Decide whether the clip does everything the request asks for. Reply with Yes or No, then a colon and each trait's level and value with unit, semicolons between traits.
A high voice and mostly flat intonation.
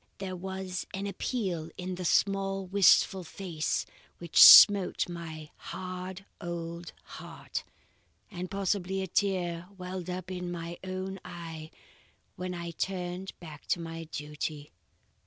No: medium, 180 Hz; narrow, 2.1 semitones